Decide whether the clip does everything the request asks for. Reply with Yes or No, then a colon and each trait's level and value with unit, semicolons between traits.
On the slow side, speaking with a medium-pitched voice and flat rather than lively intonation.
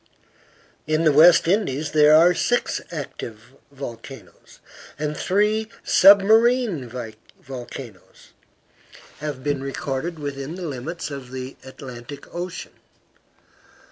No: slow, 100 wpm; medium, 150 Hz; average, 4.9 semitones